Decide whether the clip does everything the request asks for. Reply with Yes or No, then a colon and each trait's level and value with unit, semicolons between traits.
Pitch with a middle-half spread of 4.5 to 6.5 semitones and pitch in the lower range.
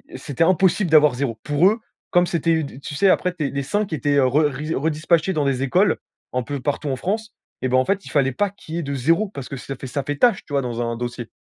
No: average, 4.8 semitones; medium, 145 Hz